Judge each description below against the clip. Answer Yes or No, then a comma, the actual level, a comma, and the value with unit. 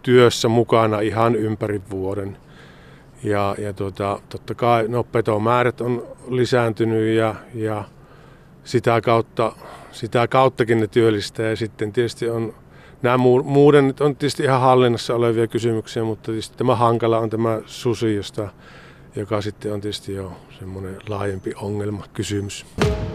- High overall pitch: No, low, 115 Hz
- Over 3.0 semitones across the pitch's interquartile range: No, narrow, 2.5 semitones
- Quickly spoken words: No, average, 130 wpm